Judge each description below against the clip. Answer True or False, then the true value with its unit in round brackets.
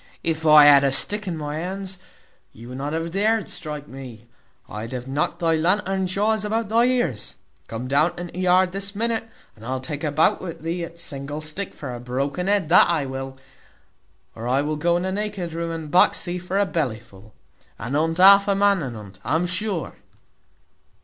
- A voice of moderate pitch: True (165 Hz)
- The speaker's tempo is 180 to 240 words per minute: True (200 wpm)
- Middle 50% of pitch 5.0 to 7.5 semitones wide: True (5.6 semitones)